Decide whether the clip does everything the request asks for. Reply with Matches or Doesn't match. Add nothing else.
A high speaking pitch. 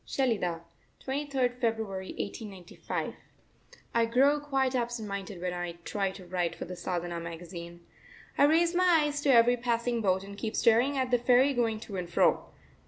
Matches